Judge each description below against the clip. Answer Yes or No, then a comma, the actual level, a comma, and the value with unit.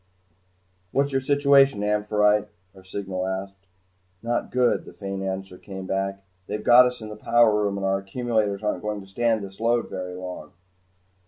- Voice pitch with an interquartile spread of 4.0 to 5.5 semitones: No, average, 3.4 semitones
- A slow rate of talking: No, average, 170 wpm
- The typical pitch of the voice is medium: No, low, 105 Hz